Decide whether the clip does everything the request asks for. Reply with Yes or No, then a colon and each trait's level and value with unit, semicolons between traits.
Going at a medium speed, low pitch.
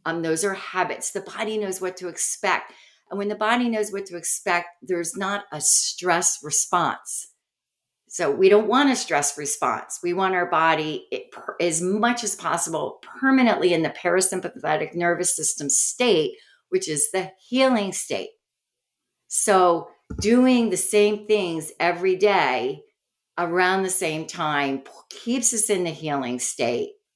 No: average, 150 wpm; high, 190 Hz